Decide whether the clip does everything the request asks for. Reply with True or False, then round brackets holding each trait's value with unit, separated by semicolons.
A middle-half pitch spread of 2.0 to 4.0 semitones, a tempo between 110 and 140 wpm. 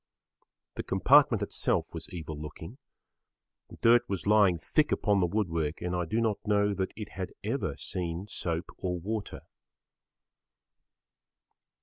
True (3.7 semitones; 135 wpm)